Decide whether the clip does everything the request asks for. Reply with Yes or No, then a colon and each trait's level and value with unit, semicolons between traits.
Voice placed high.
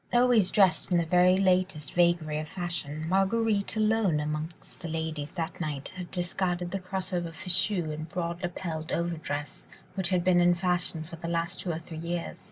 No: medium, 175 Hz